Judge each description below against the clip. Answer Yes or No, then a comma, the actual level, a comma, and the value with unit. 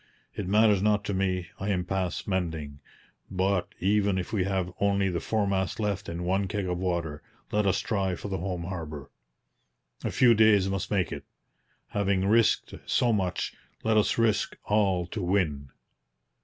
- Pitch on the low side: Yes, very low, 95 Hz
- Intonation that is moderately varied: No, narrow, 2.3 semitones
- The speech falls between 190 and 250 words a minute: No, average, 170 wpm